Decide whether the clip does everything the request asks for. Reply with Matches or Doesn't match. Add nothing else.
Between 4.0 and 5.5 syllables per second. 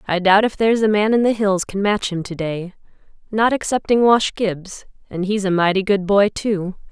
Matches